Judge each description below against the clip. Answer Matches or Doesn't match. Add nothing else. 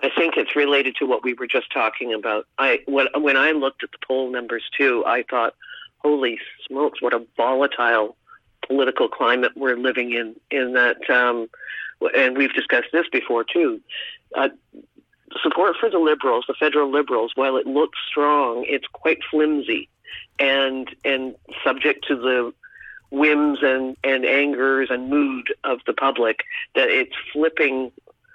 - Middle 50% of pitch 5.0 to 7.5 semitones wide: Doesn't match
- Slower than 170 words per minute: Matches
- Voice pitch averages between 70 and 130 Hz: Doesn't match